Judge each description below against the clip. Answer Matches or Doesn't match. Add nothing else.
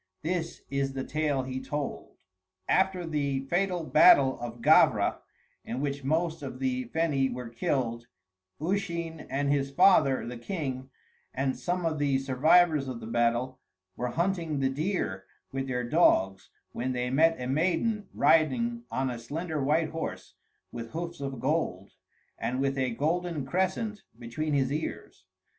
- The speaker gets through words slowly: Doesn't match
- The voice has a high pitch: Doesn't match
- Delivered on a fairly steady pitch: Doesn't match